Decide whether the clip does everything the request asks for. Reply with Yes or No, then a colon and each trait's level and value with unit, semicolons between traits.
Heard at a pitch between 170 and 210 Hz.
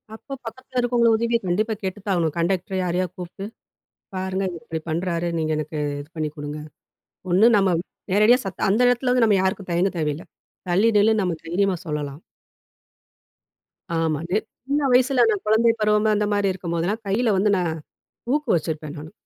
Yes: high, 190 Hz